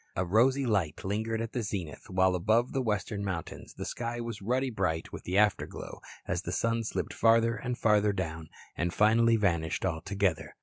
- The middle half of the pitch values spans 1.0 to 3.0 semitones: No, average, 3.8 semitones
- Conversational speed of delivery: Yes, average, 180 wpm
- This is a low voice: Yes, low, 105 Hz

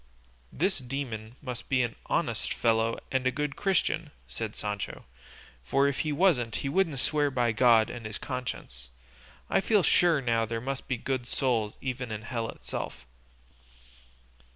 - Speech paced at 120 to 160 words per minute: Yes, average, 155 wpm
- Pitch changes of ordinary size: Yes, average, 3.8 semitones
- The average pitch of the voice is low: Yes, low, 125 Hz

